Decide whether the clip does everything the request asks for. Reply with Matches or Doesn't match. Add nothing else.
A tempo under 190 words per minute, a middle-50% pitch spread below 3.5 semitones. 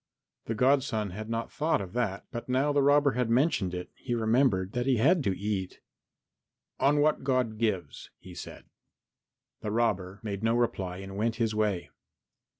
Doesn't match